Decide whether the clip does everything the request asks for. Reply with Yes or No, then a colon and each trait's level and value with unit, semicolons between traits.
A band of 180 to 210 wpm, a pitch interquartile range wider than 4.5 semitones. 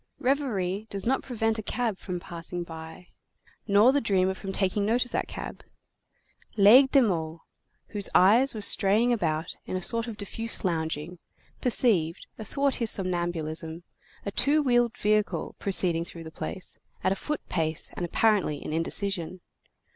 No: average, 155 wpm; average, 4.9 semitones